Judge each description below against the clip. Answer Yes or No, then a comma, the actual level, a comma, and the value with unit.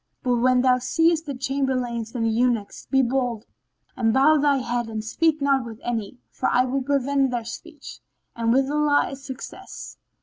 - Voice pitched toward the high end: Yes, very high, 255 Hz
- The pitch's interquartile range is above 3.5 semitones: No, average, 2.8 semitones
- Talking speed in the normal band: Yes, average, 180 wpm